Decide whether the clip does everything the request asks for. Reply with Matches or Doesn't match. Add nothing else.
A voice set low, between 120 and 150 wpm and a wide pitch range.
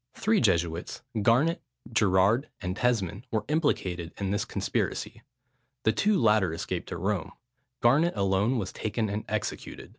Doesn't match